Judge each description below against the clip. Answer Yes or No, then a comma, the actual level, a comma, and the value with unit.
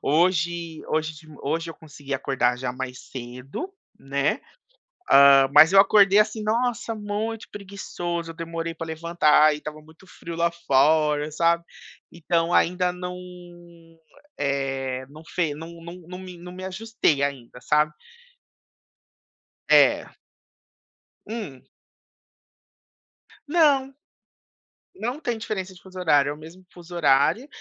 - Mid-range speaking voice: Yes, medium, 165 Hz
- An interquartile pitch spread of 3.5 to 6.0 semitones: Yes, average, 4.2 semitones